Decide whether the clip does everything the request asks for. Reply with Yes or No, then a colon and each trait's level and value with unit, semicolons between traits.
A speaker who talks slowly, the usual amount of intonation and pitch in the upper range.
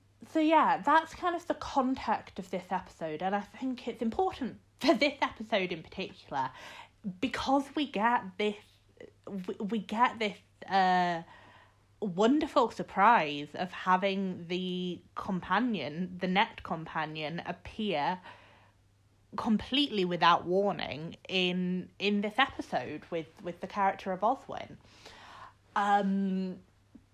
Yes: slow, 115 wpm; average, 4.6 semitones; high, 195 Hz